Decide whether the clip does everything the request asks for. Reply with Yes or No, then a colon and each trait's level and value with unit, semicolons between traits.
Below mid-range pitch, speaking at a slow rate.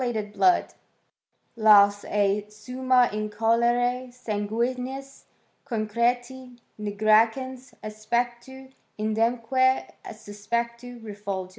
No: high, 235 Hz; slow, 95 wpm